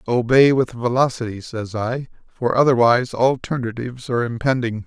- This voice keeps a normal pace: No, slow, 125 wpm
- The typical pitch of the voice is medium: No, low, 120 Hz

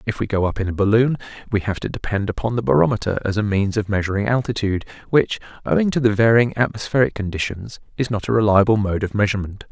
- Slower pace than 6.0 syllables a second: No, 6.7 syllables/s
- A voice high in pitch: No, low, 105 Hz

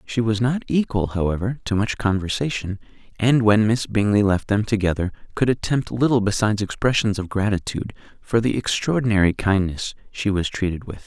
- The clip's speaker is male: Yes, male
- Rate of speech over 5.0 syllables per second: Yes, 5.5 syllables/s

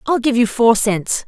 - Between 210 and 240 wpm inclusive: Yes, fast, 235 wpm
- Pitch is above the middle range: Yes, high, 235 Hz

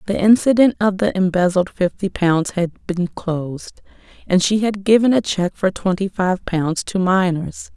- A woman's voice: Yes, female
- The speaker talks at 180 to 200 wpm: No, average, 170 wpm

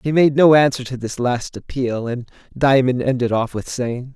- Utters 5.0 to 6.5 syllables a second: No, 4.8 syllables/s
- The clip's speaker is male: Yes, male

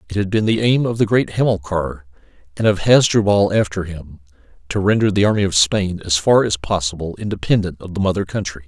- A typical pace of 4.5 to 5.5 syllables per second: No, 5.8 syllables/s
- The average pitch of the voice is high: No, very low, 95 Hz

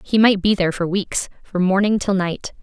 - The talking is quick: Yes, fast, 230 wpm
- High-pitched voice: Yes, high, 195 Hz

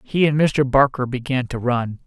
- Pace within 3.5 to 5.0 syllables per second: Yes, 4.7 syllables/s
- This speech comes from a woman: No, male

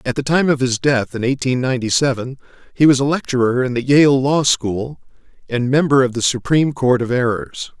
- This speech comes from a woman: No, male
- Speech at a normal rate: No, fast, 210 wpm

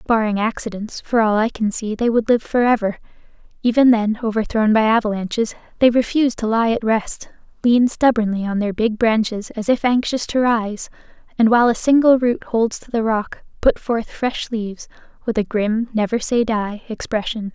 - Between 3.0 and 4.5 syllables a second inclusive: No, 5.1 syllables/s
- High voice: Yes, high, 225 Hz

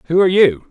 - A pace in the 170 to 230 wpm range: No, fast, 255 wpm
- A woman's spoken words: No, male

